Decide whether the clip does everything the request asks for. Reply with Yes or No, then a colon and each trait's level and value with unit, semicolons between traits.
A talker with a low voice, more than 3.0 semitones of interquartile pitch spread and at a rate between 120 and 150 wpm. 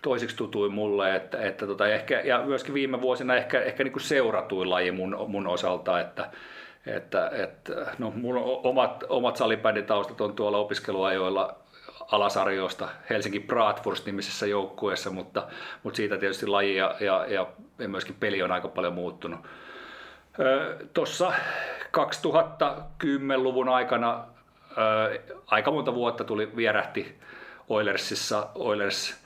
Yes: low, 110 Hz; average, 4.2 semitones; average, 125 wpm